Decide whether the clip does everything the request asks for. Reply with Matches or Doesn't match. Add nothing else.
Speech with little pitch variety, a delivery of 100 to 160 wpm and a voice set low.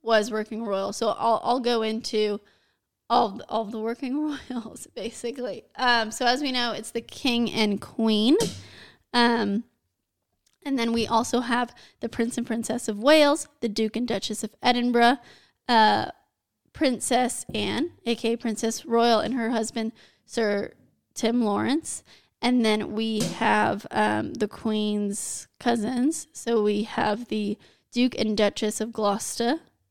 Doesn't match